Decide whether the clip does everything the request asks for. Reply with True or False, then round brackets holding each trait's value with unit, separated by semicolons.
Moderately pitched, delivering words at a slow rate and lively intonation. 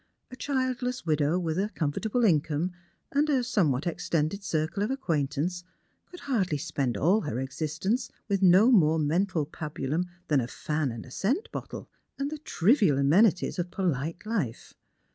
False (175 Hz; 160 wpm; 6.5 semitones)